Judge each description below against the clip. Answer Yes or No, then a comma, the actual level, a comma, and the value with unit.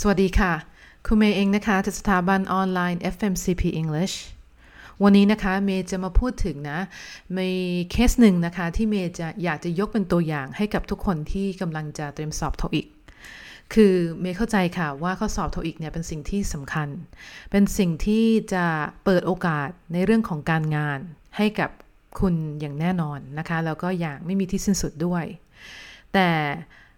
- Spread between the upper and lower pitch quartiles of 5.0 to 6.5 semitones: No, average, 3.5 semitones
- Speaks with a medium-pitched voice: Yes, medium, 180 Hz